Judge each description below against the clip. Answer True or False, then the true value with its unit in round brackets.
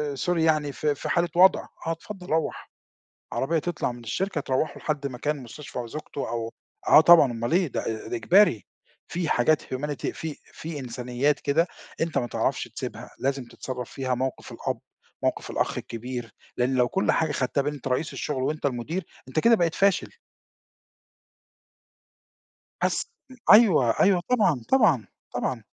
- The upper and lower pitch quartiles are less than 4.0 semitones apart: False (4.8 semitones)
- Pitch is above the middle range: False (145 Hz)